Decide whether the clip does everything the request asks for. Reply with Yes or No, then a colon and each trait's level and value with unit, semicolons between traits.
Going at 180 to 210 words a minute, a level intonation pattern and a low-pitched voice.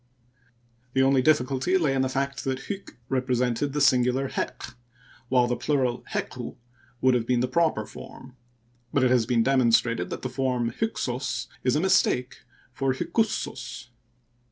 No: average, 155 wpm; narrow, 1.8 semitones; low, 130 Hz